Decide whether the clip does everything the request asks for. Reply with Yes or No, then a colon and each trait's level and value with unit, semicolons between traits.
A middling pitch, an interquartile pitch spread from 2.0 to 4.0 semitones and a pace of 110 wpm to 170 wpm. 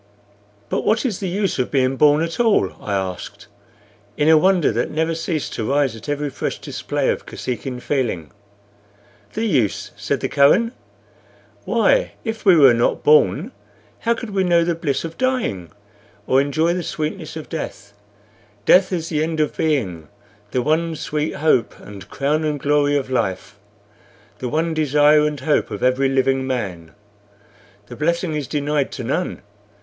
No: medium, 150 Hz; average, 4.4 semitones; average, 165 wpm